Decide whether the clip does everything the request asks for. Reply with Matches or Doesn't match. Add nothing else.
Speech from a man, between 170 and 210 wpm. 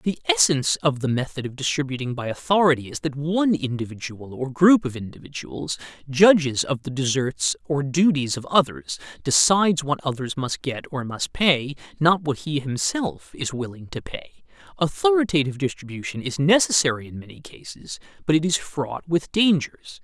Doesn't match